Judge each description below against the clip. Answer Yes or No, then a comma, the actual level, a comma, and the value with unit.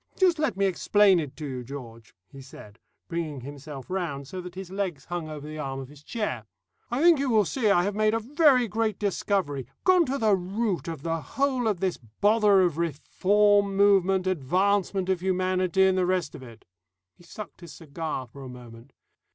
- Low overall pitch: No, medium, 185 Hz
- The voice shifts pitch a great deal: Yes, wide, 6.0 semitones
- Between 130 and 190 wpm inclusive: No, average, 200 wpm